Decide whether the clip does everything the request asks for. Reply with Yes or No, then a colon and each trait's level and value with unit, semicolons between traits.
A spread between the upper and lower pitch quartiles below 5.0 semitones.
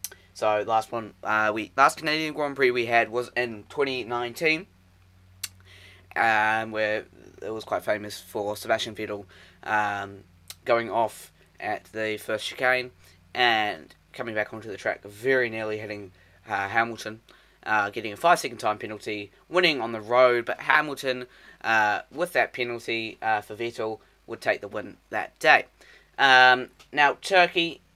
Yes: average, 3.5 semitones